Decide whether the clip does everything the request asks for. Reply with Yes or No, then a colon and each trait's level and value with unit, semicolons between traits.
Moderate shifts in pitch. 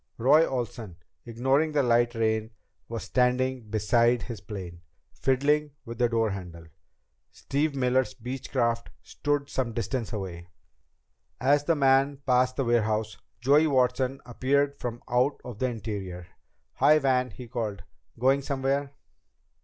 Yes: average, 3.2 semitones